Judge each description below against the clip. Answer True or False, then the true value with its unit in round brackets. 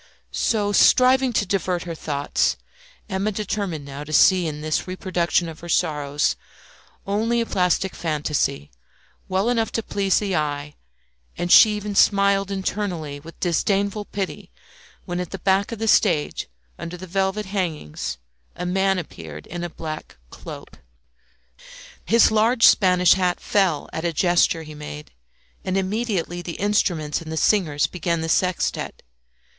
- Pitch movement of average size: True (4.0 semitones)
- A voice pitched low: False (180 Hz)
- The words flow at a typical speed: True (150 wpm)